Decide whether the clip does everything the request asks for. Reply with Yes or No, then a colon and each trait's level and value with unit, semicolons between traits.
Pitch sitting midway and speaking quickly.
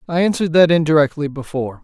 No: medium, 155 Hz; average, 165 wpm